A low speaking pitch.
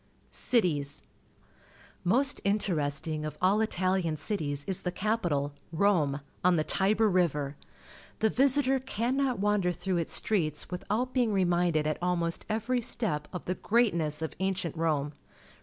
No: medium, 180 Hz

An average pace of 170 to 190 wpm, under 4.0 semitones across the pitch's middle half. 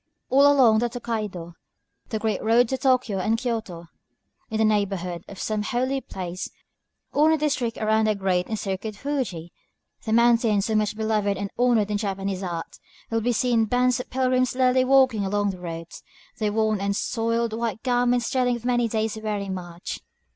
Yes: average, 180 wpm; average, 3.5 semitones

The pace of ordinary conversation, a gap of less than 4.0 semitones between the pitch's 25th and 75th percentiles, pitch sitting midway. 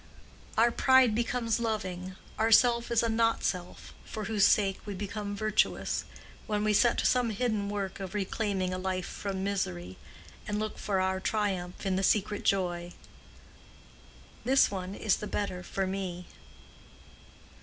No: average, 150 wpm; average, 2.7 semitones; high, 205 Hz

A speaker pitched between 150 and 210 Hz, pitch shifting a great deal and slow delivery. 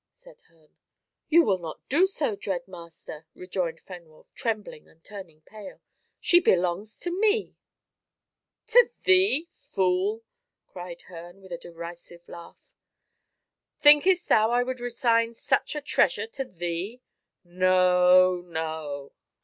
Yes: medium, 185 Hz; wide, 6.4 semitones; slow, 125 wpm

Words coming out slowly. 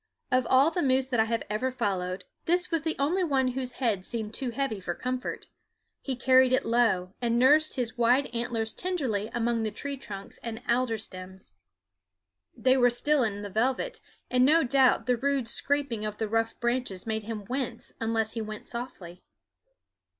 No: average, 180 wpm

